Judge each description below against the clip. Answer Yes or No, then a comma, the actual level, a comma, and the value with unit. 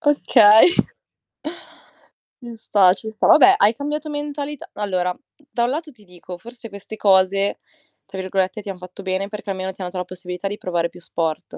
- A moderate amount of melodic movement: Yes, average, 4.2 semitones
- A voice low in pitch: No, high, 200 Hz